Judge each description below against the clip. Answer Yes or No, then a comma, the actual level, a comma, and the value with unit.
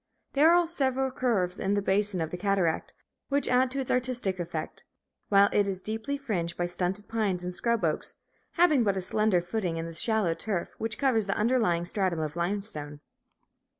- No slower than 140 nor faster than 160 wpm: No, average, 185 wpm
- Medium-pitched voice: No, high, 200 Hz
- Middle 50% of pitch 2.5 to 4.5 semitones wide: No, wide, 5.5 semitones